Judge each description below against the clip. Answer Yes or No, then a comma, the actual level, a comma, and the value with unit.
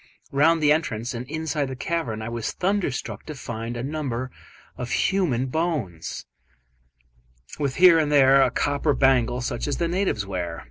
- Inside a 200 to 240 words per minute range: No, average, 160 wpm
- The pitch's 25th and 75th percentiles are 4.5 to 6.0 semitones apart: Yes, average, 5.1 semitones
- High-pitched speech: No, low, 135 Hz